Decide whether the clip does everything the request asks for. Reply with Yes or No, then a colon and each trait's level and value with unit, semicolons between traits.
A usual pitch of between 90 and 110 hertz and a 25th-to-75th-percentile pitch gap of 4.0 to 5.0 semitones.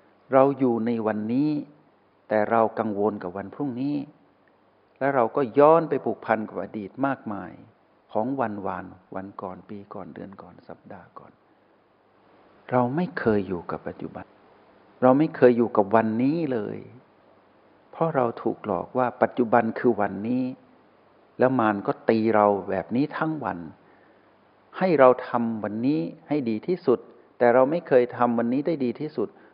No: low, 120 Hz; average, 4.5 semitones